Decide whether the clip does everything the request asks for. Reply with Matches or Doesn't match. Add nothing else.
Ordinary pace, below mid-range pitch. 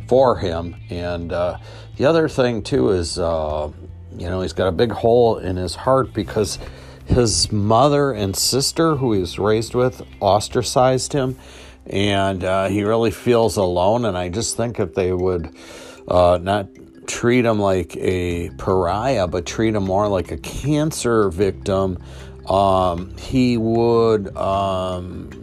Matches